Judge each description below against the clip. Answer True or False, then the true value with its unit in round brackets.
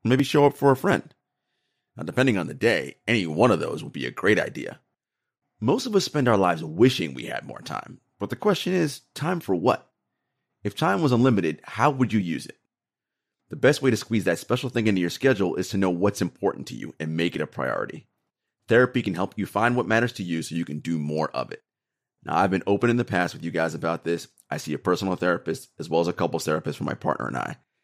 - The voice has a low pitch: True (95 Hz)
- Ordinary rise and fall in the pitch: False (7.2 semitones)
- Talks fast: True (245 wpm)